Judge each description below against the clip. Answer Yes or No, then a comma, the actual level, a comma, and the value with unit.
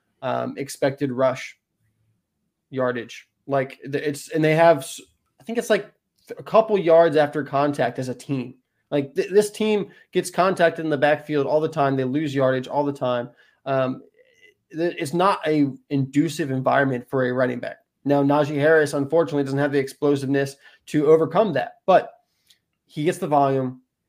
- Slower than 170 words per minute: Yes, average, 160 wpm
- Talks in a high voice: No, medium, 145 Hz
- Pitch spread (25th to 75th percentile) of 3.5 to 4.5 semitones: Yes, average, 3.8 semitones